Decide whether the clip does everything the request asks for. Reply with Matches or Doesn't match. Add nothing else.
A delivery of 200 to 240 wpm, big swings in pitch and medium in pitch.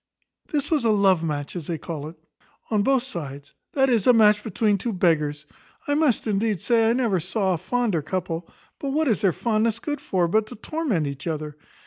Doesn't match